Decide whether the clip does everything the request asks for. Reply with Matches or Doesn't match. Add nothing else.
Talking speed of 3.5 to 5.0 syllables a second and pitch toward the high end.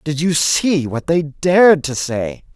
Doesn't match